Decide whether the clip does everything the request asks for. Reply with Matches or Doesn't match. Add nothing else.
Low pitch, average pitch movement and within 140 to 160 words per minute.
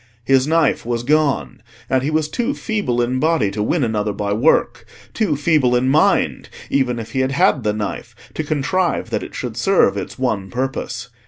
Doesn't match